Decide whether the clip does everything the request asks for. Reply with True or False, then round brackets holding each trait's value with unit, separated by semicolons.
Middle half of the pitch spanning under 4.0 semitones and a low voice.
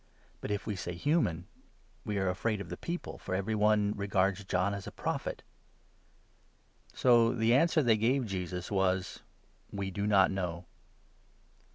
True (3.2 semitones; 100 Hz)